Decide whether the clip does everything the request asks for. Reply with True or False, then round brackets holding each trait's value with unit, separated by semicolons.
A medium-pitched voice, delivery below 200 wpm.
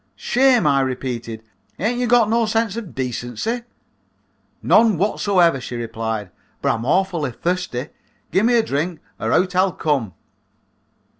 True (175 Hz; 145 wpm)